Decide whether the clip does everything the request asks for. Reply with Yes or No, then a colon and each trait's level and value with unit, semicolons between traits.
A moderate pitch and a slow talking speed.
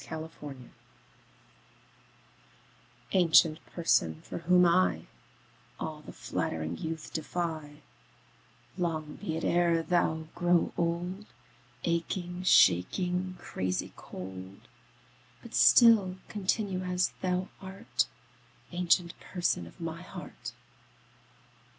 Yes: medium, 170 Hz; slow, 95 wpm